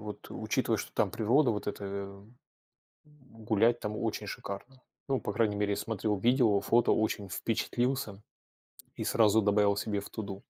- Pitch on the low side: Yes, low, 105 Hz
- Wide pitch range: No, average, 2.7 semitones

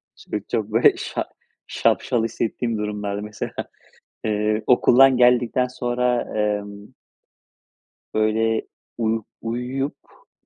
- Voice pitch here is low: Yes, low, 115 Hz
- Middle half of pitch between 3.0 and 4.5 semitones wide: No, narrow, 2.5 semitones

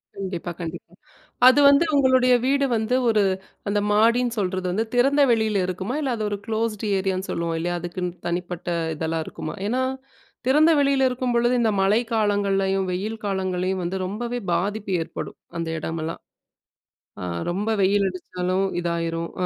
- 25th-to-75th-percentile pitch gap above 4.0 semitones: Yes, average, 4.7 semitones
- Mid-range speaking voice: No, high, 200 Hz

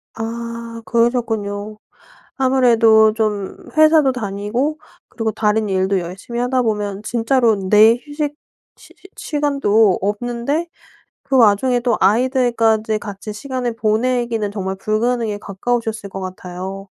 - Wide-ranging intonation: No, average, 3.0 semitones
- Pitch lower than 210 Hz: No, high, 225 Hz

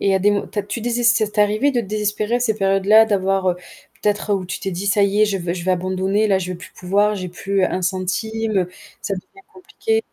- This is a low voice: No, high, 200 Hz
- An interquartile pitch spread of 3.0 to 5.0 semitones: No, narrow, 2.6 semitones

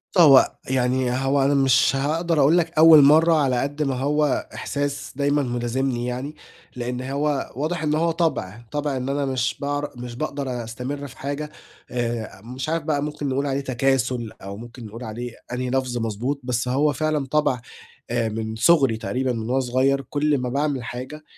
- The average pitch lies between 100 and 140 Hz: Yes, low, 135 Hz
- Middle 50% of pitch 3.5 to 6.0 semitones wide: No, average, 2.9 semitones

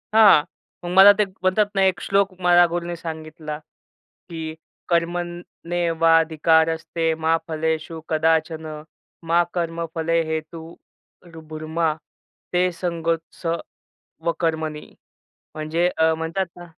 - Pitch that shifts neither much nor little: No, narrow, 1.5 semitones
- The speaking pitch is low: No, medium, 165 Hz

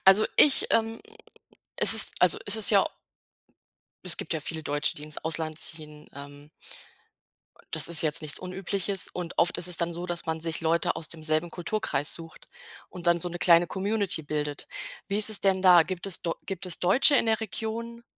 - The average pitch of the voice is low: No, medium, 175 Hz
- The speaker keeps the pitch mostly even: No, average, 3.6 semitones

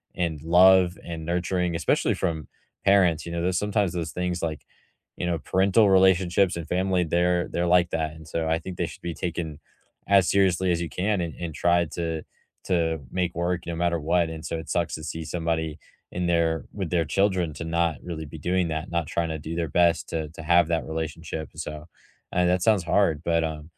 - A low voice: Yes, very low, 85 Hz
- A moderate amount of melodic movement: No, narrow, 1.7 semitones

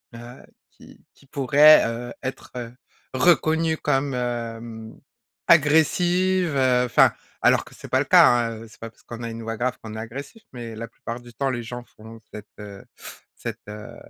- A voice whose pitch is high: No, low, 120 Hz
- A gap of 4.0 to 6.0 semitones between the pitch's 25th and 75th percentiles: No, average, 3.4 semitones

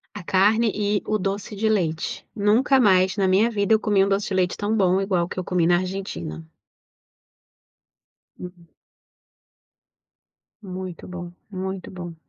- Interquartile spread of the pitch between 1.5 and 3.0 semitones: Yes, narrow, 2.4 semitones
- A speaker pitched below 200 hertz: Yes, high, 190 Hz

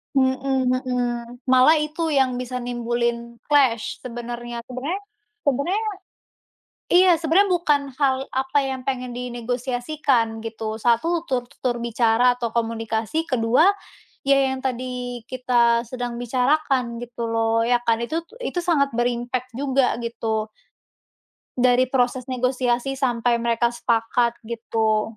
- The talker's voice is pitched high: Yes, high, 245 Hz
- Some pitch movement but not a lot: No, narrow, 2.1 semitones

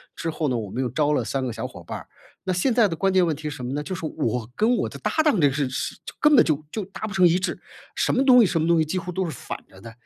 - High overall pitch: No, medium, 160 Hz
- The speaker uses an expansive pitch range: Yes, wide, 5.9 semitones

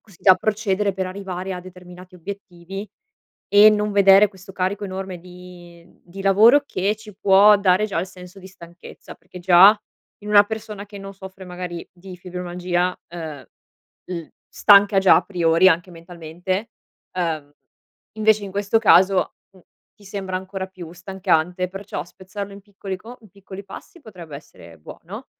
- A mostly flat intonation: Yes, narrow, 2.1 semitones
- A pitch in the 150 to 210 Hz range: Yes, high, 190 Hz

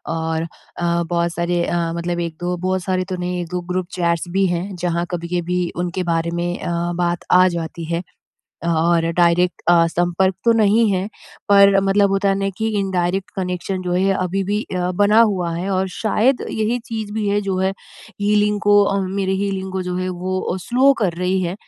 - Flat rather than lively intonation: Yes, narrow, 2.3 semitones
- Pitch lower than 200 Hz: Yes, medium, 185 Hz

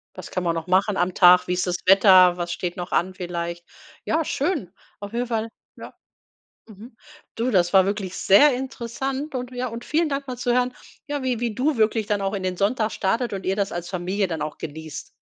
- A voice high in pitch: Yes, high, 200 Hz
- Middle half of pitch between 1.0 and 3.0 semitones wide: No, wide, 5.5 semitones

